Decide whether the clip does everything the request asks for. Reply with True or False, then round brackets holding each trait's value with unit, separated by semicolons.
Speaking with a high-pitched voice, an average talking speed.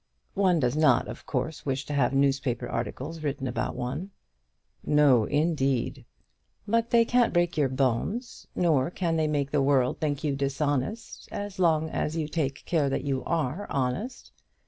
False (145 Hz; 165 wpm)